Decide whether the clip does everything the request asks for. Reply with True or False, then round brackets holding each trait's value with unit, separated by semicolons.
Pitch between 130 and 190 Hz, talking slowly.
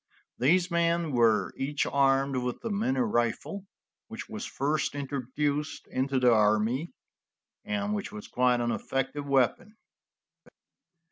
True (140 Hz; 125 wpm)